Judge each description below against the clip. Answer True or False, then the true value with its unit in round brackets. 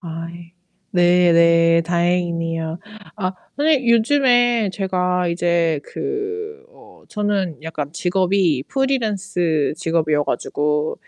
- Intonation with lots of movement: False (4.6 semitones)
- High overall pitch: False (175 Hz)